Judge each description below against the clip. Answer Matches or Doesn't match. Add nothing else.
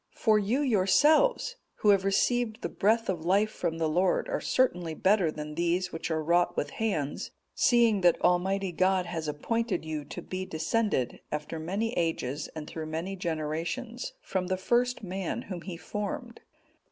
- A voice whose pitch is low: Doesn't match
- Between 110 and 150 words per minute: Doesn't match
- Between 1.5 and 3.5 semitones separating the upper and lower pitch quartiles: Doesn't match